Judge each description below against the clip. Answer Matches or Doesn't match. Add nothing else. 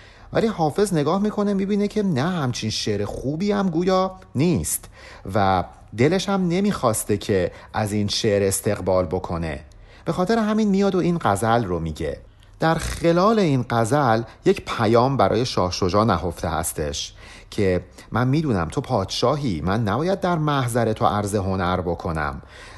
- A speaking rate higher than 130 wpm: Matches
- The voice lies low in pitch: Matches